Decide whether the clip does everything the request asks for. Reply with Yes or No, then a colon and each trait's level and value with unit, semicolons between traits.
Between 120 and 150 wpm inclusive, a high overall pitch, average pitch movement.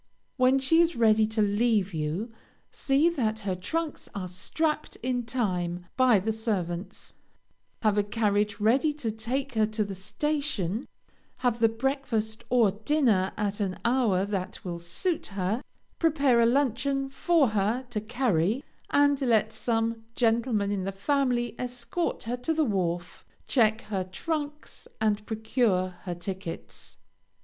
Yes: average, 145 wpm; high, 225 Hz; average, 4.6 semitones